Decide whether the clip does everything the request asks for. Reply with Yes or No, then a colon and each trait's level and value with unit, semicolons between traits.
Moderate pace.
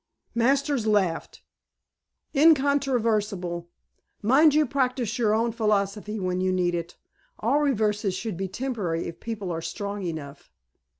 No: slow, 125 wpm